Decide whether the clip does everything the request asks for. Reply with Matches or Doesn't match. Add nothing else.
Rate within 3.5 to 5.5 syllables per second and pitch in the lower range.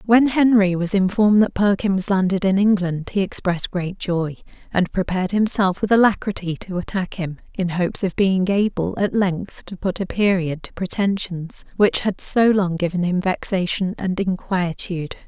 Doesn't match